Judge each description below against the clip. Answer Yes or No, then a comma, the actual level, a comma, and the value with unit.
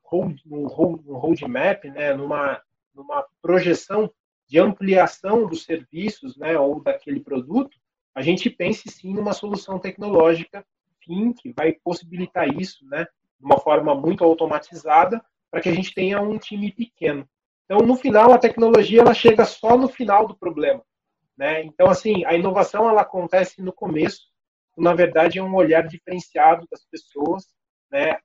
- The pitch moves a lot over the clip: No, average, 4.8 semitones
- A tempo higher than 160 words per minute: No, average, 155 wpm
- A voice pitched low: No, medium, 185 Hz